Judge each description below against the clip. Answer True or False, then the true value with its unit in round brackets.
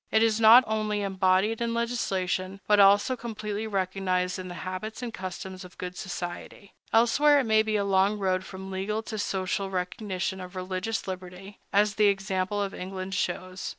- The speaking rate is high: False (175 wpm)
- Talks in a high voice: True (195 Hz)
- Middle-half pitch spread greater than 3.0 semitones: False (2.7 semitones)